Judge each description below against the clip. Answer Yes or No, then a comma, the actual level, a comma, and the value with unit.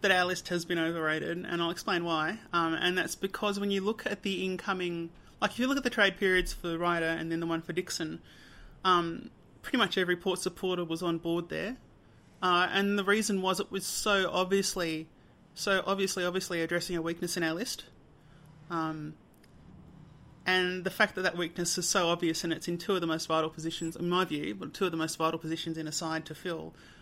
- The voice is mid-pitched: Yes, medium, 175 Hz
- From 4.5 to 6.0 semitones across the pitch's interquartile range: No, narrow, 2.6 semitones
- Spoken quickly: Yes, fast, 220 wpm